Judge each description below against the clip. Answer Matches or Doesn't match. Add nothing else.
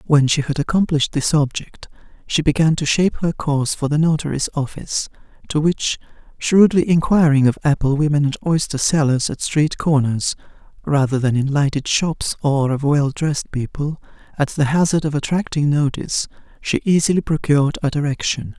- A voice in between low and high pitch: Matches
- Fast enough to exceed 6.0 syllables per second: Doesn't match